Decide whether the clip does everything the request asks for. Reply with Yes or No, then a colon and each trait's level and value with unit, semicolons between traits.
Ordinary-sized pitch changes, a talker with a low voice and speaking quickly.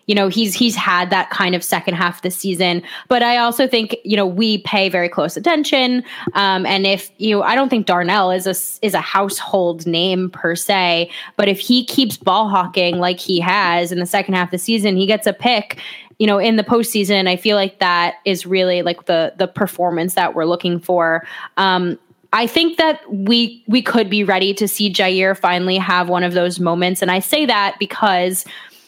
No: average, 3.1 semitones; high, 195 Hz; fast, 215 wpm